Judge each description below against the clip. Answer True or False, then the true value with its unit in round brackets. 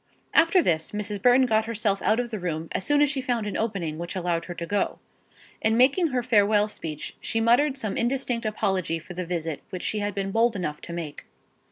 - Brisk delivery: True (220 wpm)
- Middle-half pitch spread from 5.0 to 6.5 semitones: True (5.3 semitones)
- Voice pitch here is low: False (210 Hz)